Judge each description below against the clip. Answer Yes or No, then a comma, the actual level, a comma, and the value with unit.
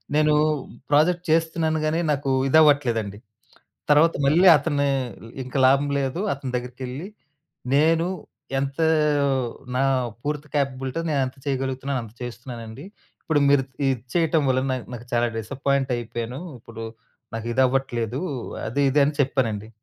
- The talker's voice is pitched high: No, low, 135 Hz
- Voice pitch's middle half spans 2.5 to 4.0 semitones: Yes, average, 3.2 semitones